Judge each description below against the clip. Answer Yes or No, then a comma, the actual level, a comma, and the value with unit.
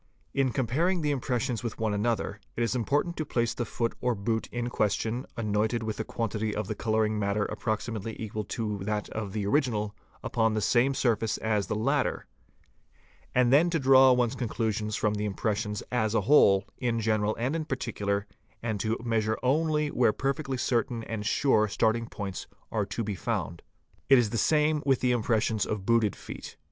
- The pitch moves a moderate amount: Yes, average, 3.0 semitones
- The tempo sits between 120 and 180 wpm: No, average, 190 wpm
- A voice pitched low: Yes, low, 115 Hz